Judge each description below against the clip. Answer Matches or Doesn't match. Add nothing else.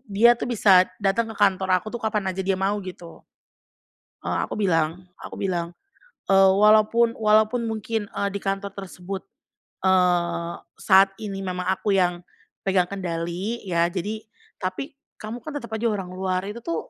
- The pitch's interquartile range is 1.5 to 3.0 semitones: Matches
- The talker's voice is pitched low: Doesn't match